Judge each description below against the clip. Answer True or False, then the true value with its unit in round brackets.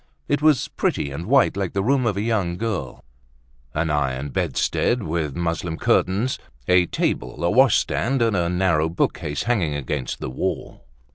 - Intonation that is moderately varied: False (6.8 semitones)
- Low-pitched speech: True (90 Hz)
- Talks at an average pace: True (160 wpm)